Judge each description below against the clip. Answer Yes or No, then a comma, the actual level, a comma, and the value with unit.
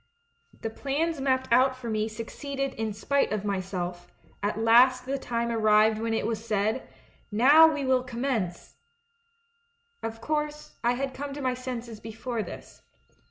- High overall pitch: Yes, high, 245 Hz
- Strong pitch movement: No, average, 4.0 semitones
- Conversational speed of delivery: Yes, average, 160 wpm